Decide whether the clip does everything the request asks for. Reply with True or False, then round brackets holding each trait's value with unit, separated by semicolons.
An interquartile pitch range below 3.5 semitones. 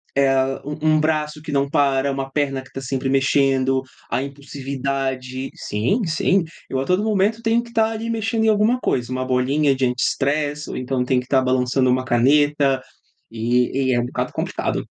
True (2.9 semitones)